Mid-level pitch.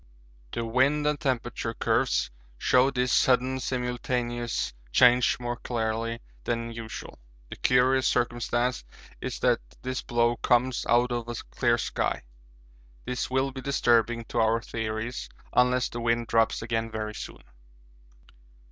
No: low, 120 Hz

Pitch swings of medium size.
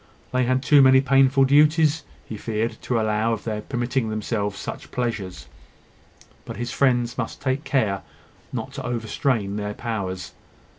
Yes: average, 3.6 semitones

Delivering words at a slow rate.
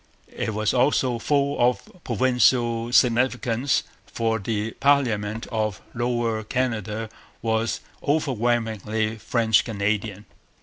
Yes: slow, 95 wpm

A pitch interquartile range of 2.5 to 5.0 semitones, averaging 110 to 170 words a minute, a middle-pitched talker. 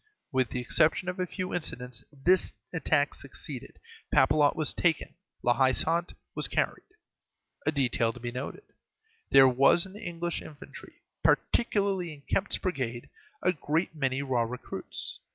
No: wide, 5.6 semitones; average, 150 wpm; medium, 150 Hz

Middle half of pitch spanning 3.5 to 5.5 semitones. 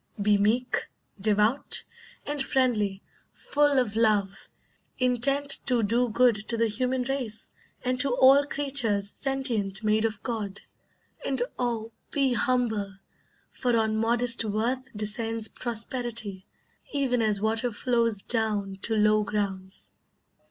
No: average, 3.1 semitones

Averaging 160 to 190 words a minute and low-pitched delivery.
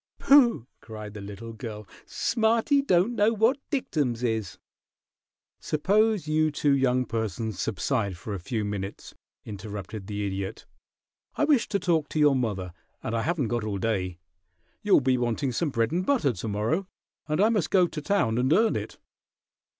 Yes: average, 165 wpm; low, 125 Hz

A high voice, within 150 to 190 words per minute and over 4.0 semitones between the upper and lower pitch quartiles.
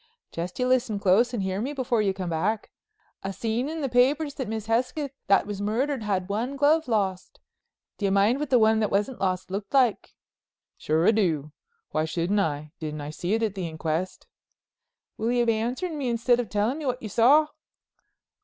No: high, 220 Hz; average, 200 wpm; average, 4.9 semitones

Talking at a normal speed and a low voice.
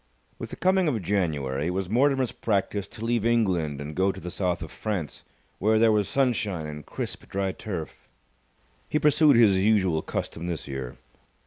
Yes: average, 180 wpm; very low, 95 Hz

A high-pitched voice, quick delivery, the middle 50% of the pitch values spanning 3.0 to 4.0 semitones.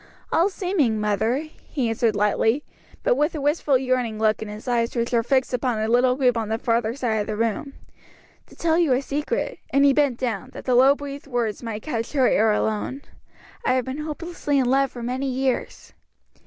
Yes: very high, 255 Hz; fast, 210 wpm; average, 3.7 semitones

